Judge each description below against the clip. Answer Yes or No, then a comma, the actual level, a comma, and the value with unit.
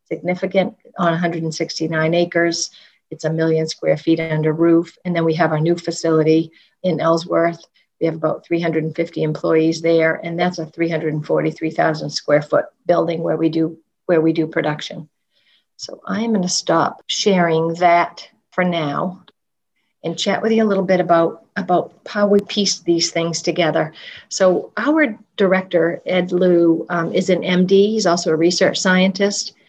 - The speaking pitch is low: No, medium, 170 Hz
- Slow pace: No, average, 160 wpm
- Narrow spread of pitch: Yes, narrow, 2.3 semitones